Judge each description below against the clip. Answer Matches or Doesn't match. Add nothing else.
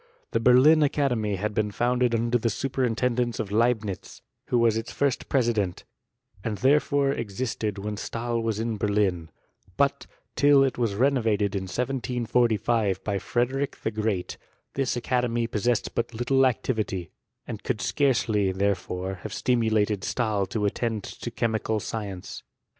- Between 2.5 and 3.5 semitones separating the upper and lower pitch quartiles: Matches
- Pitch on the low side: Matches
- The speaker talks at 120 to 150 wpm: Matches